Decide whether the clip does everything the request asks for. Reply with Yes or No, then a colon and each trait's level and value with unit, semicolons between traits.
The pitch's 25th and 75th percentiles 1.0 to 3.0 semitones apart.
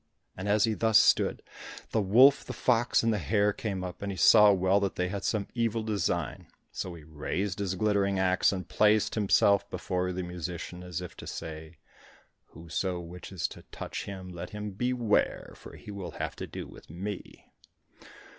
Yes: average, 2.7 semitones